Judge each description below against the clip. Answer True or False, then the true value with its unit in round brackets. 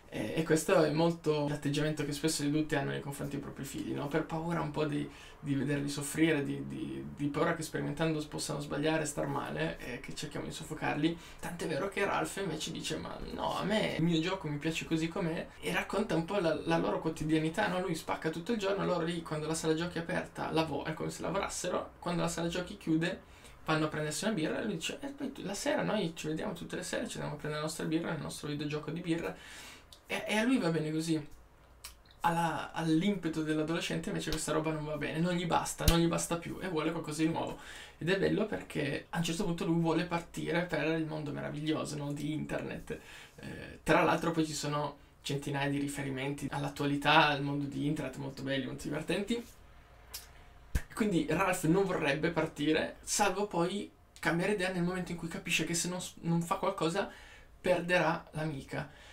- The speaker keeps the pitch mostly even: True (2.3 semitones)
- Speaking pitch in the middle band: True (160 Hz)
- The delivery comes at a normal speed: False (205 wpm)